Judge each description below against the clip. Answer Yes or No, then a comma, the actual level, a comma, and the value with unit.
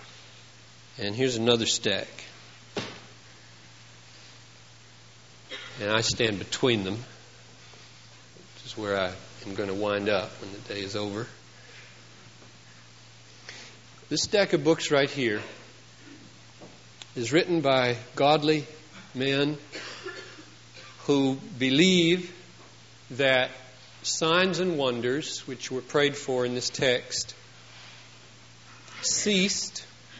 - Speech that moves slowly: Yes, slow, 95 wpm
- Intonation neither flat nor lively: Yes, average, 3.6 semitones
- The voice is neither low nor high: No, low, 125 Hz